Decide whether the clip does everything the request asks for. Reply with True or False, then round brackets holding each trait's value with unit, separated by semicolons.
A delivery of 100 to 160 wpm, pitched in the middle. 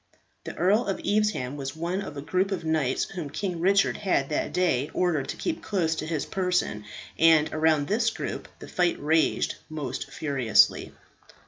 False (175 wpm; 160 Hz)